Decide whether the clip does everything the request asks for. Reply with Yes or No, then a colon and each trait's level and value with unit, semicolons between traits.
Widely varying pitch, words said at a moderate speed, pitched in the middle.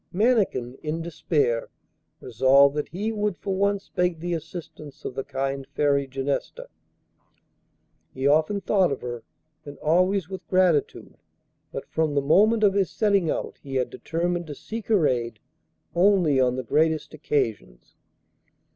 Yes: wide, 5.7 semitones; average, 145 wpm; medium, 160 Hz